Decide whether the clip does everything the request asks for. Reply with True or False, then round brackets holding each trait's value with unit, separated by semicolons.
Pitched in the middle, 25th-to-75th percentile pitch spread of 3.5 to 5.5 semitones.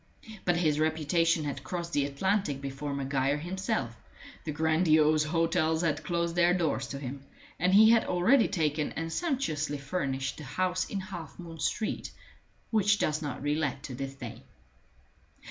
True (155 Hz; 3.8 semitones)